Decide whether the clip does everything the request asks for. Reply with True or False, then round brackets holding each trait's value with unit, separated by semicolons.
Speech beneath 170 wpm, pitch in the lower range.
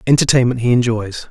True (140 wpm; 120 Hz)